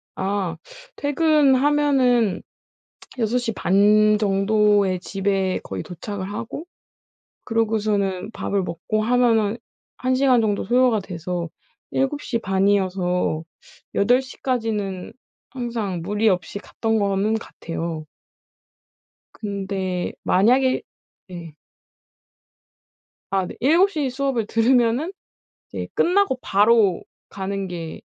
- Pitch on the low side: No, high, 210 Hz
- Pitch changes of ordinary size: Yes, average, 4.5 semitones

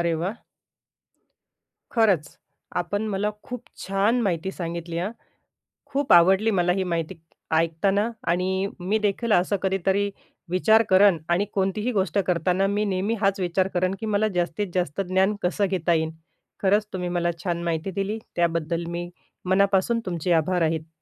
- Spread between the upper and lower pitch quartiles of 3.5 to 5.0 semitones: No, average, 2.8 semitones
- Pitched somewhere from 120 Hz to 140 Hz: No, medium, 185 Hz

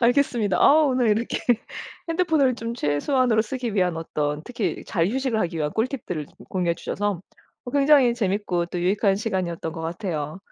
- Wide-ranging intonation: Yes, wide, 6.4 semitones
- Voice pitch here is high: Yes, high, 210 Hz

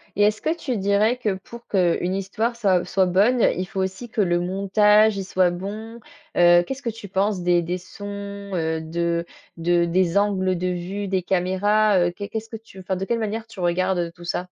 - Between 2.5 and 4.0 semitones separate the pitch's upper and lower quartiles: Yes, average, 2.9 semitones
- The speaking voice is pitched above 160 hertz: Yes, high, 190 Hz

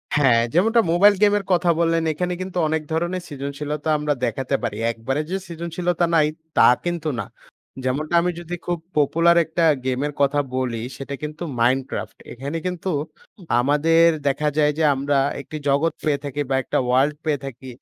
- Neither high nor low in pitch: Yes, medium, 150 Hz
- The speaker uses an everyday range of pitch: Yes, average, 3.8 semitones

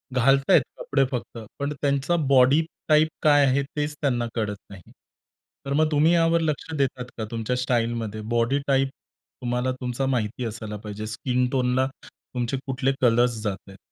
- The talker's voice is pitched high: No, low, 130 Hz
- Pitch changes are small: No, average, 3.2 semitones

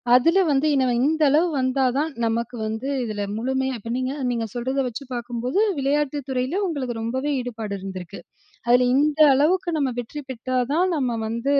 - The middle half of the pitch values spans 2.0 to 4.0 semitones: Yes, average, 3.6 semitones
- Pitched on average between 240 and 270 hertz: Yes, very high, 260 Hz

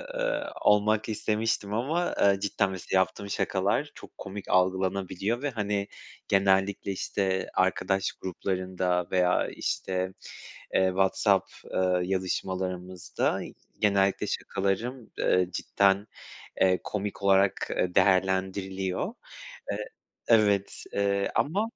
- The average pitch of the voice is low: Yes, very low, 95 Hz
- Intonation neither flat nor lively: No, narrow, 1.6 semitones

